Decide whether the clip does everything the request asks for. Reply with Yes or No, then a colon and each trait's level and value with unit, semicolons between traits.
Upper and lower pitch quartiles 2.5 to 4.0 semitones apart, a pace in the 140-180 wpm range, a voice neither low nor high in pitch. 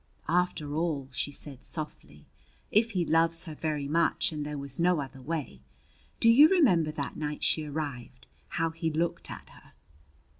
Yes: average, 2.8 semitones; average, 165 wpm; medium, 155 Hz